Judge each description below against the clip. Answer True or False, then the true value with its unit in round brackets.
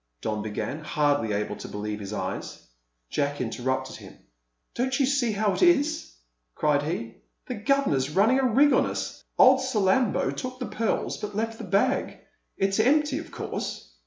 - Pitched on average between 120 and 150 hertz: False (205 Hz)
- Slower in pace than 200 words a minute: True (165 wpm)